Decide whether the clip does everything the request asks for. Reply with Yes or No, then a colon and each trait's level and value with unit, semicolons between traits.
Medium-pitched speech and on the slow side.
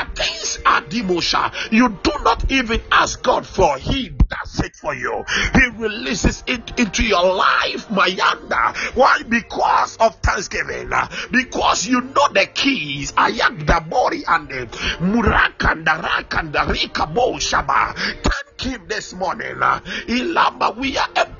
No: high, 235 Hz; slow, 130 wpm